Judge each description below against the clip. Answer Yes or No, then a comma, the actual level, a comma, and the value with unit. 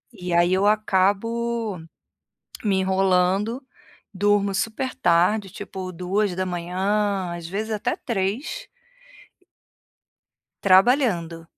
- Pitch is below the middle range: No, high, 195 Hz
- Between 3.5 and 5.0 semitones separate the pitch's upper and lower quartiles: No, average, 2.8 semitones